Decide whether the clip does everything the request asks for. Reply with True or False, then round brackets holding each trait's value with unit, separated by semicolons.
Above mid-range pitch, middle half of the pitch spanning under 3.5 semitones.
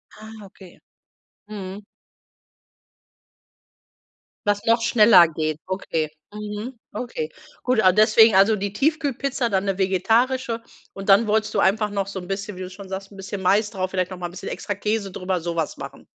True (200 Hz; 2.7 semitones)